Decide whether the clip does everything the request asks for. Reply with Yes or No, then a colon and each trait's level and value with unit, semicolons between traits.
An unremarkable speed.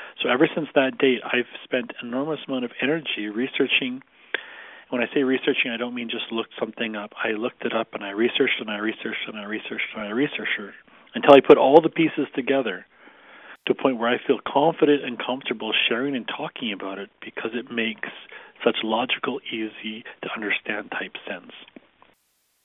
Yes: average, 185 wpm